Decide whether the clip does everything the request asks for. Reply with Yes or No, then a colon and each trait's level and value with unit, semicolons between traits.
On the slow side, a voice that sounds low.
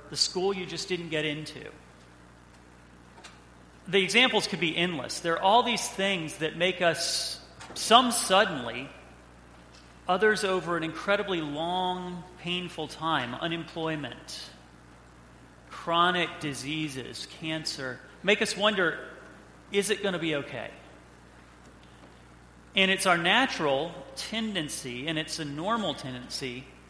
No: slow, 115 wpm; medium, 160 Hz